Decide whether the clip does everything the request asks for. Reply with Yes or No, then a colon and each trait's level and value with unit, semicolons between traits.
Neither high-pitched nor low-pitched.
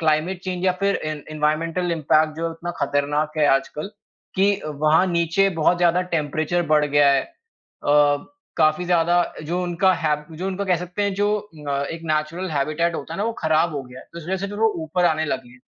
Yes: medium, 160 Hz